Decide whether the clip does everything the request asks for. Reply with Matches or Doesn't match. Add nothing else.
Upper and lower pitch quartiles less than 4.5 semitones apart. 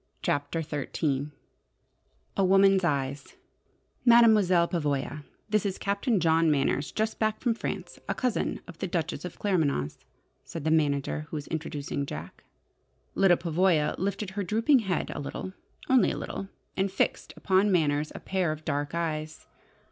Doesn't match